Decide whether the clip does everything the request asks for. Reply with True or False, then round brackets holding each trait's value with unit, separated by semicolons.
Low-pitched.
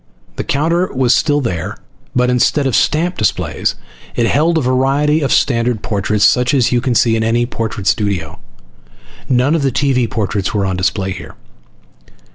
True (125 Hz)